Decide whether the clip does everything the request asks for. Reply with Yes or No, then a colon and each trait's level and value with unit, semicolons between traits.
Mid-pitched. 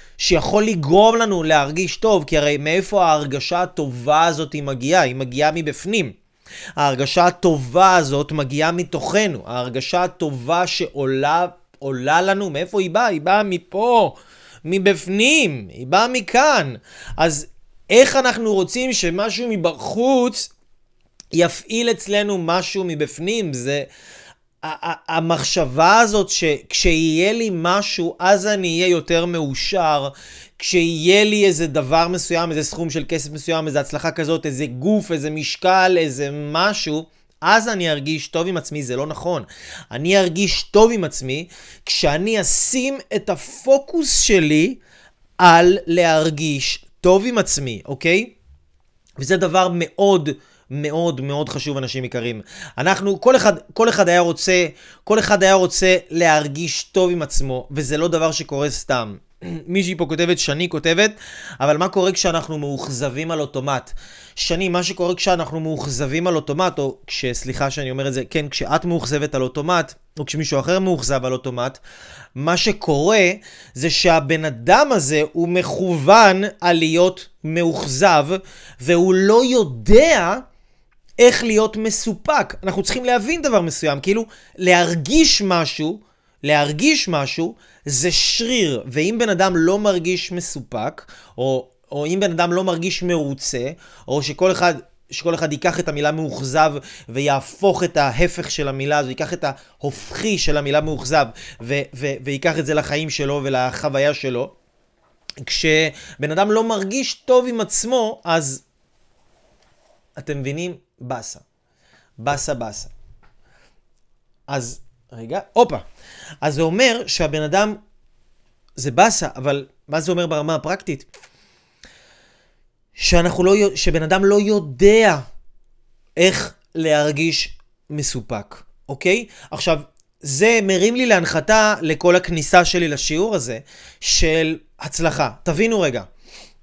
Yes: medium, 165 Hz